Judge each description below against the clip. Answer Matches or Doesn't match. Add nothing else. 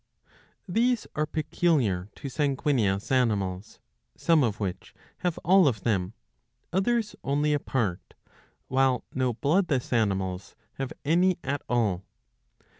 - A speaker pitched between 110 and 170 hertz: Matches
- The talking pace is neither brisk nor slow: Doesn't match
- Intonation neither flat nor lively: Doesn't match